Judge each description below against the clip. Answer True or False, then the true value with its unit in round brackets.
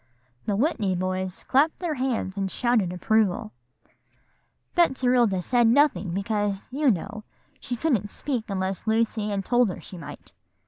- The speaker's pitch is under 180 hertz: False (215 Hz)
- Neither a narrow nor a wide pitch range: True (4.7 semitones)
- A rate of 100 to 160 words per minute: True (145 wpm)